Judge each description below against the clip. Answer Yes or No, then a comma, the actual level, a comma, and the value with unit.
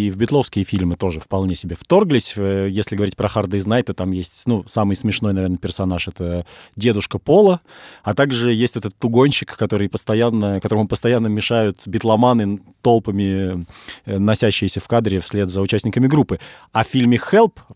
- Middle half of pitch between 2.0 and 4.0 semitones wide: Yes, average, 3.5 semitones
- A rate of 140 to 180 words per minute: Yes, fast, 160 wpm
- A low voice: Yes, low, 105 Hz